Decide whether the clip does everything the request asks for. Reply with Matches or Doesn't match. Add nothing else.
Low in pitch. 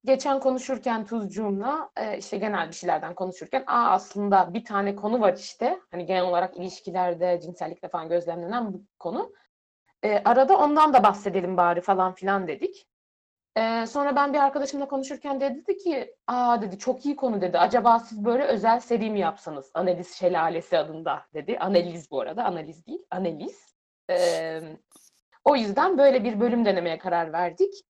Doesn't match